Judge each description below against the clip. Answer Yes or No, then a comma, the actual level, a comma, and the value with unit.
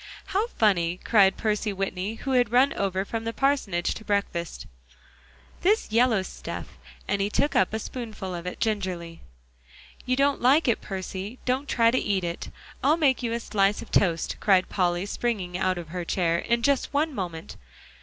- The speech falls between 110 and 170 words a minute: No, average, 185 wpm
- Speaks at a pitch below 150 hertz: No, high, 205 Hz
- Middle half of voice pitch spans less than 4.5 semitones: No, average, 4.9 semitones